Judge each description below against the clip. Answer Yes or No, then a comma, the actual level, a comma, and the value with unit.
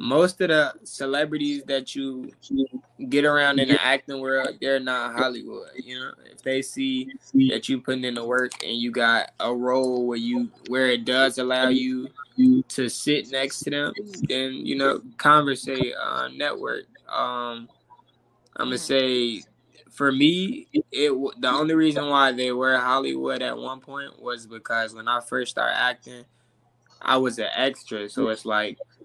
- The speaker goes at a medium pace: Yes, average, 165 wpm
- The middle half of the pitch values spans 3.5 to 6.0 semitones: No, average, 3.1 semitones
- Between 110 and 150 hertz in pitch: Yes, low, 135 Hz